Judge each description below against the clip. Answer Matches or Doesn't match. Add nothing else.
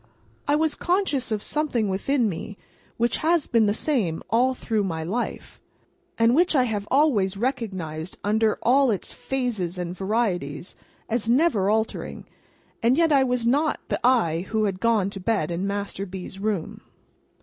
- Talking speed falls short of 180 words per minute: Matches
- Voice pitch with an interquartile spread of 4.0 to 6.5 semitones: Matches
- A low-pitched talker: Doesn't match